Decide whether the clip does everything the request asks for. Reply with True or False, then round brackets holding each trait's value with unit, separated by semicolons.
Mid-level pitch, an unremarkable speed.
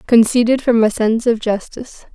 False (230 Hz; 170 wpm)